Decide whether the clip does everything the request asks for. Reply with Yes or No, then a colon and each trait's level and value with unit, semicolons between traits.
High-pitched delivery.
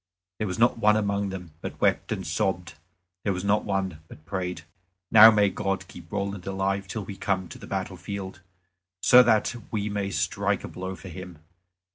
No: very low, 95 Hz